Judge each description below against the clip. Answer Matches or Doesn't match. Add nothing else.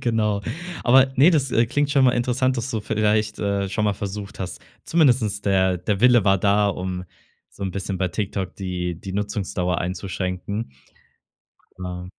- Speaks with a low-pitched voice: Matches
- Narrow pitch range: Doesn't match